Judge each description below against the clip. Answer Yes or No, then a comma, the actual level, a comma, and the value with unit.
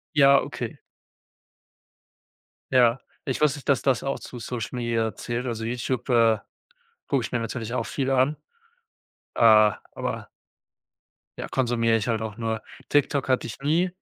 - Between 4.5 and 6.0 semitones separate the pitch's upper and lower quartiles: No, average, 2.9 semitones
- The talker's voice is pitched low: Yes, low, 120 Hz